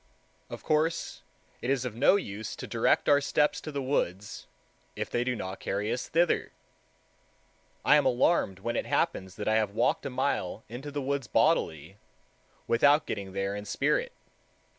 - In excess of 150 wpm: Yes, average, 170 wpm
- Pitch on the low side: Yes, low, 120 Hz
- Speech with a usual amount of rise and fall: No, wide, 6.0 semitones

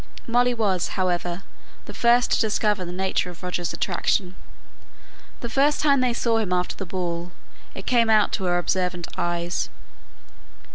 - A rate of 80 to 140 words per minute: No, average, 155 wpm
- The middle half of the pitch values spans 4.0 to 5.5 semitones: Yes, average, 4.6 semitones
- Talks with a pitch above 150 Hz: Yes, high, 190 Hz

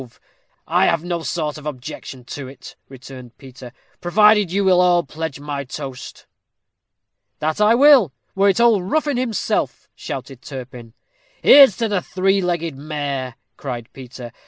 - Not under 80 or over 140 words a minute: No, average, 155 wpm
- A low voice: No, medium, 155 Hz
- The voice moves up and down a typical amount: No, wide, 6.6 semitones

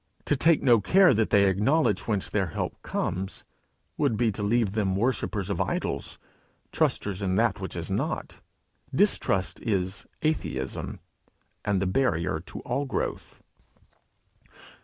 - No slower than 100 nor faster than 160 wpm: Yes, slow, 135 wpm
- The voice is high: No, low, 105 Hz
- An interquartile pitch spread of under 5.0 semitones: Yes, average, 4.2 semitones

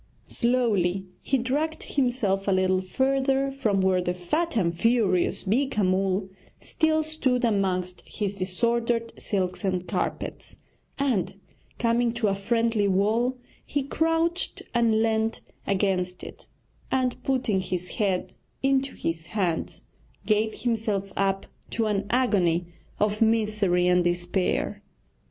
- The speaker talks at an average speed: No, slow, 125 wpm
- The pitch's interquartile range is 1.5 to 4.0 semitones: No, average, 4.7 semitones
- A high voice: Yes, high, 215 Hz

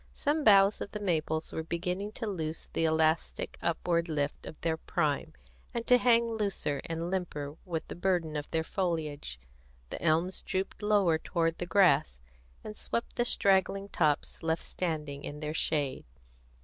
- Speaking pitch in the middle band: Yes, medium, 170 Hz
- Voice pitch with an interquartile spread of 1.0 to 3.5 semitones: No, average, 3.9 semitones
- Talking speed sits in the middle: Yes, average, 160 wpm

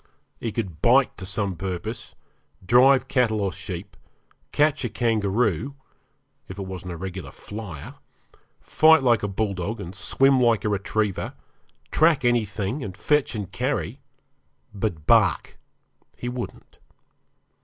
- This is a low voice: Yes, low, 105 Hz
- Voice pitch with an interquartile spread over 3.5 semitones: Yes, average, 4.5 semitones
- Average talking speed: No, slow, 130 wpm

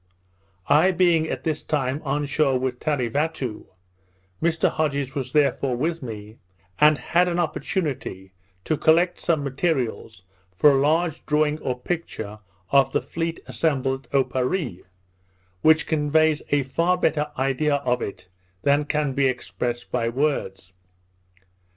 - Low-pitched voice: No, medium, 145 Hz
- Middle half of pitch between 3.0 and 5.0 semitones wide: Yes, average, 3.6 semitones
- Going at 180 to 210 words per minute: No, slow, 135 wpm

